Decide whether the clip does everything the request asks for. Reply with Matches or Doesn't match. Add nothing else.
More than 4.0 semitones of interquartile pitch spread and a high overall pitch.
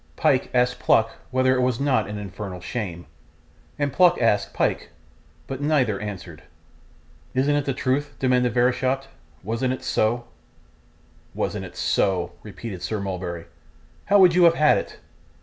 Doesn't match